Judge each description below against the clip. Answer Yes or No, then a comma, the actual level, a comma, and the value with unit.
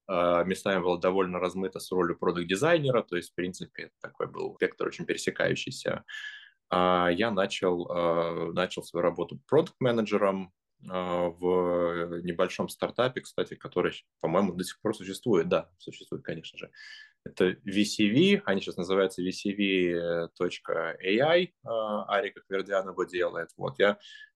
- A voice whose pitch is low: Yes, very low, 95 Hz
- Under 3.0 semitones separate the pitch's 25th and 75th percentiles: No, average, 4.0 semitones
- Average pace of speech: Yes, average, 140 wpm